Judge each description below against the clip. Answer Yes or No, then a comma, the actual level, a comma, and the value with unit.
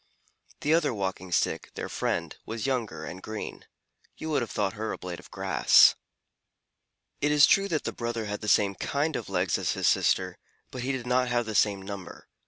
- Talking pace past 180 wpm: Yes, average, 200 wpm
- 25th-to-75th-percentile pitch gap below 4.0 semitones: No, average, 5.2 semitones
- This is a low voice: Yes, low, 110 Hz